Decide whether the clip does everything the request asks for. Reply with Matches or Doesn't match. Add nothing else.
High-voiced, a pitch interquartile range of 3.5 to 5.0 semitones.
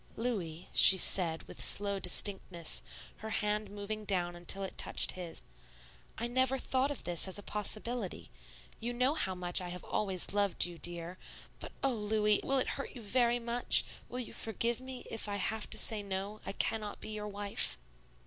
Matches